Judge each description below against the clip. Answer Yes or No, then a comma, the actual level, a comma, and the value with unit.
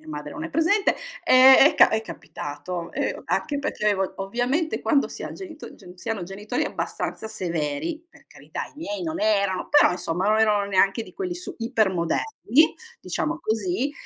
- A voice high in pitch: Yes, high, 220 Hz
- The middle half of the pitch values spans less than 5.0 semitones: No, wide, 8.6 semitones